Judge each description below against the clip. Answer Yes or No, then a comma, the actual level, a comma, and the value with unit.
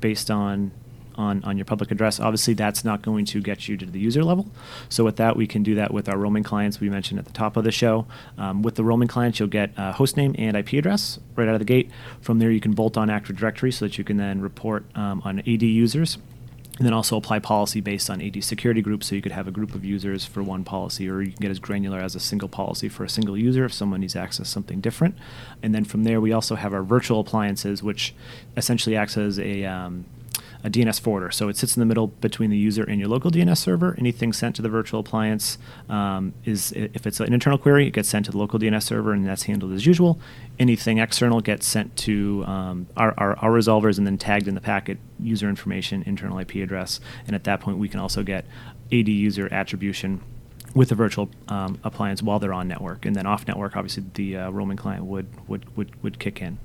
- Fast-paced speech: Yes, fast, 245 wpm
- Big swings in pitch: No, average, 2.7 semitones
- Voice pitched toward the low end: Yes, low, 110 Hz